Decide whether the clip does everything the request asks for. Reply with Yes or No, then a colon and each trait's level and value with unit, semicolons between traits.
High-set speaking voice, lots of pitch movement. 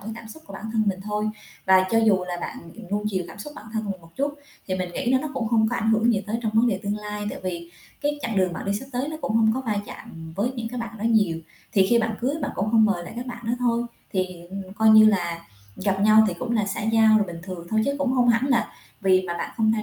No: high, 215 Hz; average, 3.4 semitones